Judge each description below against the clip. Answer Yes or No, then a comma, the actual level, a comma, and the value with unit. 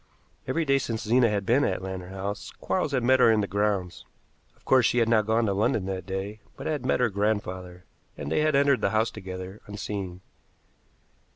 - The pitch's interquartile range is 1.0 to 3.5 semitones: No, average, 4.3 semitones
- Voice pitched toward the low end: Yes, low, 105 Hz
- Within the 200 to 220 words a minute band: Yes, fast, 205 wpm